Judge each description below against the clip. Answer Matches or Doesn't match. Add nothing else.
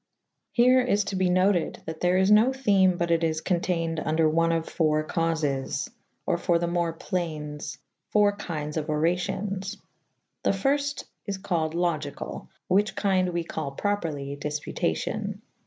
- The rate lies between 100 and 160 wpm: Matches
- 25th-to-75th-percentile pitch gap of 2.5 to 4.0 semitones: Matches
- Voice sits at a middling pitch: Matches